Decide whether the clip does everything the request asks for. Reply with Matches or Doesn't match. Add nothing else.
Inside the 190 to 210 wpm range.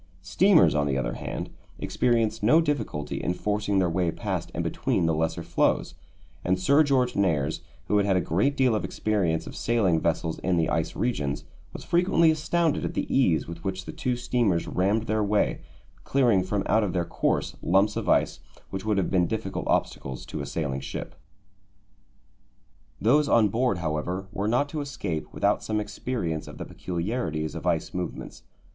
Doesn't match